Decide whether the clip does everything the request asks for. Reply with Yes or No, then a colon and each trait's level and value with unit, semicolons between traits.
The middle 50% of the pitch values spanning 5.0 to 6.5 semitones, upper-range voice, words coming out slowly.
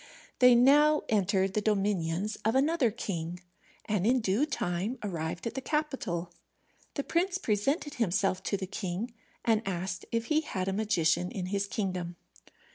No: average, 5.3 semitones; high, 205 Hz; average, 155 wpm